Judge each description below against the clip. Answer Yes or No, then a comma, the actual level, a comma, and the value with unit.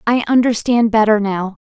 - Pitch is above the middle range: Yes, high, 220 Hz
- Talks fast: No, average, 140 wpm